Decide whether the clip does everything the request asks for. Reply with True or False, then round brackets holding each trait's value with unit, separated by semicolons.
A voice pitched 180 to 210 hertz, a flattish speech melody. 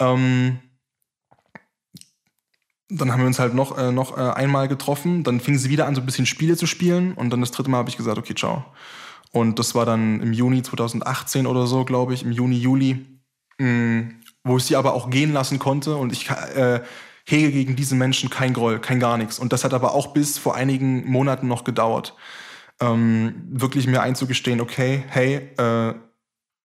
False (130 Hz; 1.8 semitones)